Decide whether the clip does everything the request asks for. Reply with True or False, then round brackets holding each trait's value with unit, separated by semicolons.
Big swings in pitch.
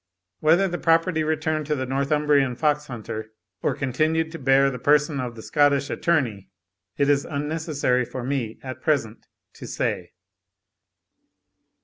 False (3.3 semitones)